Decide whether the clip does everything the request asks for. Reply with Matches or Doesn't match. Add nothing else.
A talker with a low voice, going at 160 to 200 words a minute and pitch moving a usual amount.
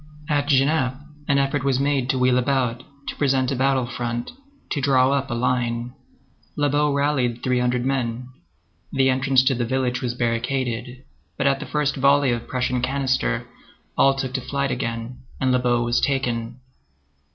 Doesn't match